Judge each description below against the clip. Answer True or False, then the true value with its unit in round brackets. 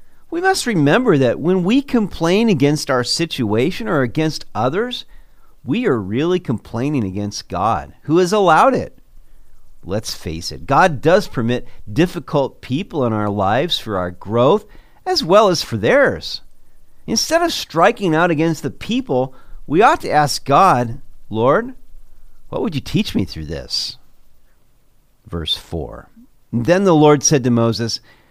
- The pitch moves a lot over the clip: True (7.7 semitones)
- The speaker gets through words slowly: False (150 wpm)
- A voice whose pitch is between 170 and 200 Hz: False (135 Hz)